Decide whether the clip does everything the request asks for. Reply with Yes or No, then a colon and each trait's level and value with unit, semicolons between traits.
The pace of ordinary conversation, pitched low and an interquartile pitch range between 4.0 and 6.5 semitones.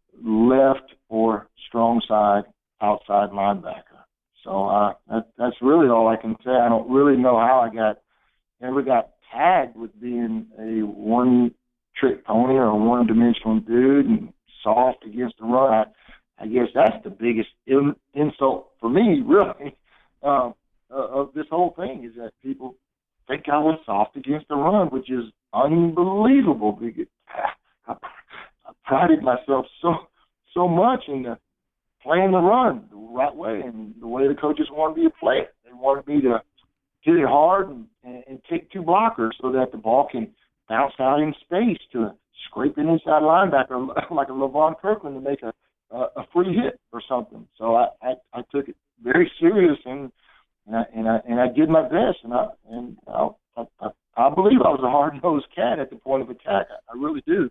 Yes: average, 185 wpm; low, 130 Hz; average, 5.3 semitones